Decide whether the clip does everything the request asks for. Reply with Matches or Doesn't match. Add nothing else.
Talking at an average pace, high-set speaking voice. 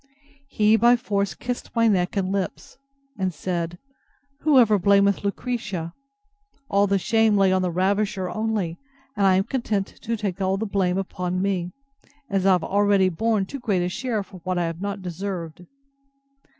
Matches